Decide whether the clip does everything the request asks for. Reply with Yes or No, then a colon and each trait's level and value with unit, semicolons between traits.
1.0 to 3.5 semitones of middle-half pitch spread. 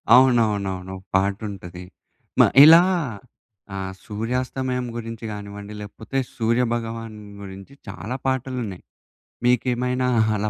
No: average, 4.0 semitones